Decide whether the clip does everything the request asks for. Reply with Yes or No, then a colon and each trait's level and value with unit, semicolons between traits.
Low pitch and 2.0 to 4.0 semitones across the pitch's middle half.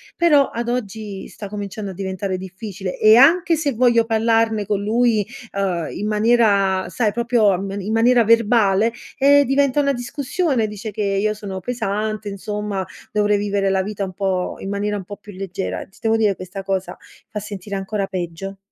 No: high, 210 Hz; average, 2.8 semitones